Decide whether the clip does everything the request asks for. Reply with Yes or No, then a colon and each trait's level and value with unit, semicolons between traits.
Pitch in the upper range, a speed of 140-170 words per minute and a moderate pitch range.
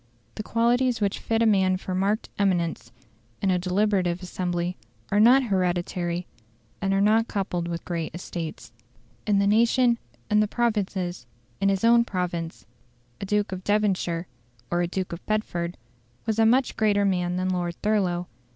Yes: high, 195 Hz; average, 160 wpm; average, 3.2 semitones